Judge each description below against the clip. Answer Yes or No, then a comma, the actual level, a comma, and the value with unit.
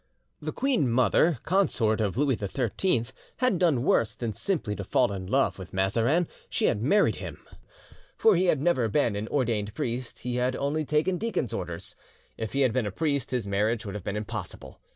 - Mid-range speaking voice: No, low, 120 Hz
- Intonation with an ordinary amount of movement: No, wide, 6.2 semitones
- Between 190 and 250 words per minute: Yes, average, 195 wpm